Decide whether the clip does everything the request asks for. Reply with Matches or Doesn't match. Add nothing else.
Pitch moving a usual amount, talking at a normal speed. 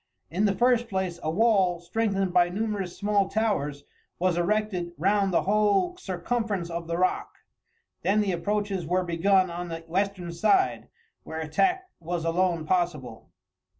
Matches